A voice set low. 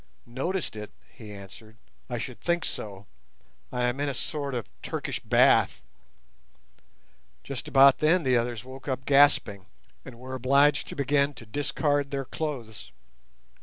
Yes: low, 130 Hz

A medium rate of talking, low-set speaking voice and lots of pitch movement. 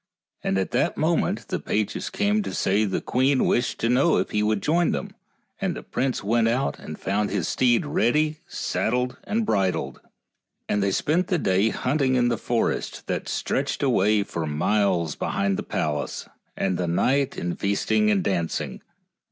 Yes: average, 175 wpm; low, 115 Hz; wide, 6.3 semitones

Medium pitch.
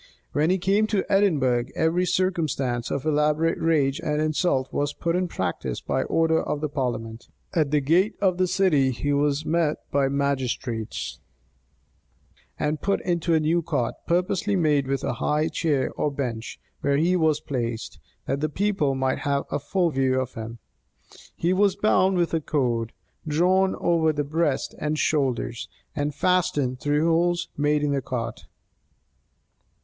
Yes: medium, 150 Hz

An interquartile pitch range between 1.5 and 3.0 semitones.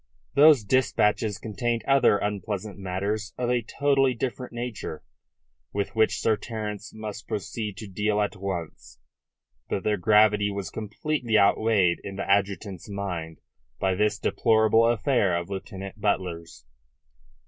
Yes: narrow, 2.4 semitones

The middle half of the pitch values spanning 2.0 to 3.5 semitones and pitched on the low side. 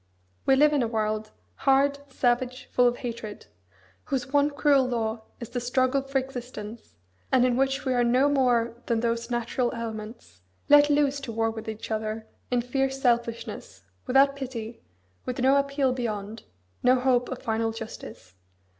No: average, 2.9 semitones; high, 245 Hz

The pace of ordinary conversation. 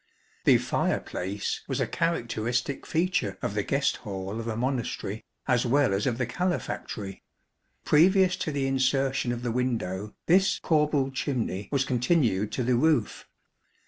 Yes: average, 145 wpm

